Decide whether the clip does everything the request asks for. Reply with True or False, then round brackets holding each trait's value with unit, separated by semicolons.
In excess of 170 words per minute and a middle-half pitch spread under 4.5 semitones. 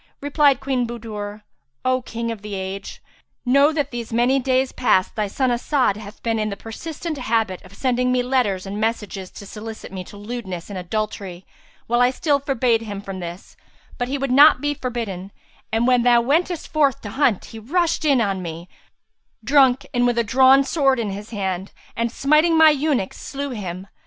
False (190 wpm; 4.8 semitones)